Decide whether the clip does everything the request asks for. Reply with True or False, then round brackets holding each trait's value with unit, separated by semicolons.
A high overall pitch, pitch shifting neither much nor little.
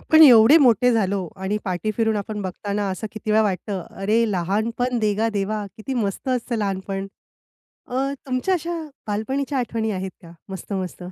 True (215 Hz; 3.8 semitones)